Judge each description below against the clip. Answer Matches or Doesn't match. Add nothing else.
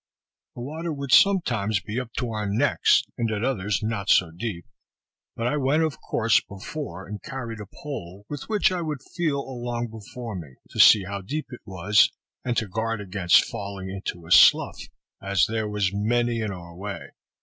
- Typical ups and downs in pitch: Matches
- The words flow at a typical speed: Matches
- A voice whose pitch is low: Matches